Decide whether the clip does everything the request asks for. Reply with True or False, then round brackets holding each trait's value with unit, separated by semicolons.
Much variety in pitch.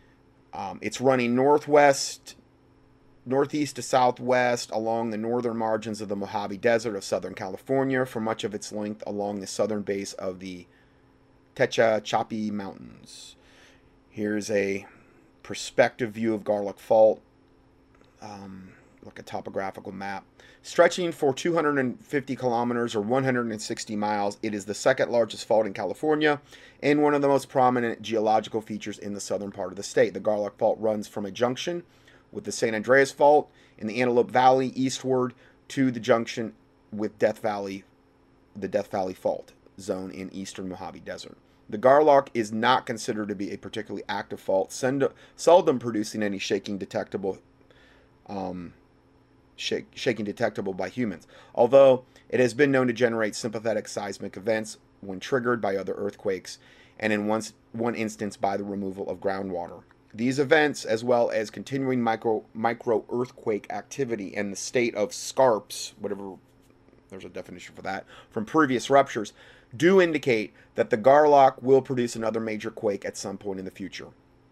False (4.2 semitones)